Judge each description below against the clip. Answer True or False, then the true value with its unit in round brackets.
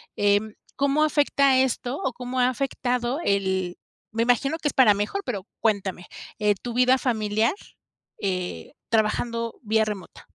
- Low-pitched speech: False (230 Hz)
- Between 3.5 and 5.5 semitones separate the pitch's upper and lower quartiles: True (3.9 semitones)